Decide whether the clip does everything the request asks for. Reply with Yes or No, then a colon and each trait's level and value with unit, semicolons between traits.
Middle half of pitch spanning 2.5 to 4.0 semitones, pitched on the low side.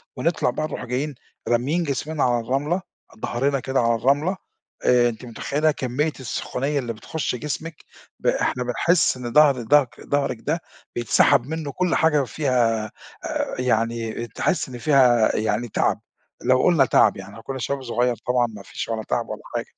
Yes: average, 3.7 semitones; low, 130 Hz